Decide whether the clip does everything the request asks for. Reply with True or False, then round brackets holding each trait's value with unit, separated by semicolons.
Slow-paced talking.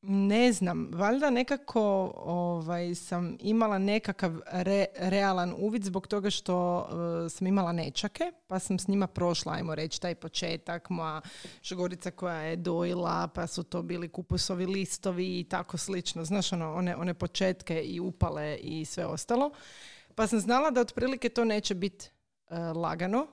False (155 wpm)